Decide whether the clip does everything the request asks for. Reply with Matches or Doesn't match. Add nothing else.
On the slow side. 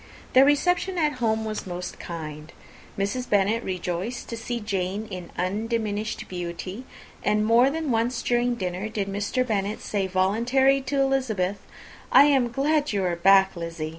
Doesn't match